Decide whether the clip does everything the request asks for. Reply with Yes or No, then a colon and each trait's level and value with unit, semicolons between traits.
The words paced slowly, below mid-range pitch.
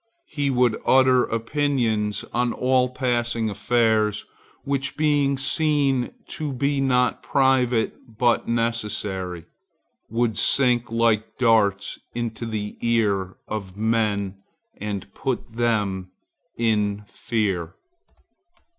Yes: slow, 100 wpm; low, 115 Hz